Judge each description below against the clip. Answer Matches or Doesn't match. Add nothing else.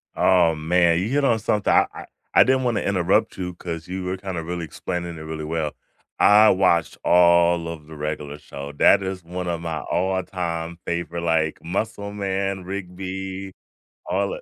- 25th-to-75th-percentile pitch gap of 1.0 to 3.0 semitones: Matches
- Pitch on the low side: Matches